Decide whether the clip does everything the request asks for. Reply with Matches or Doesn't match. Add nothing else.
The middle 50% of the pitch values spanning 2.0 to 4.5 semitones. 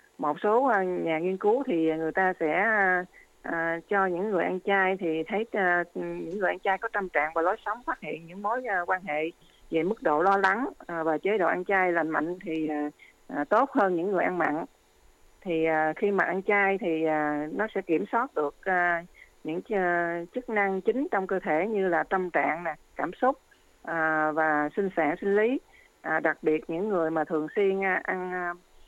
Matches